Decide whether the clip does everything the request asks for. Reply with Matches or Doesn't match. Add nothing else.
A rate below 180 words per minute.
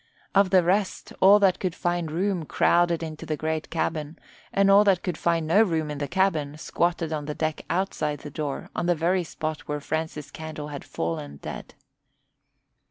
Doesn't match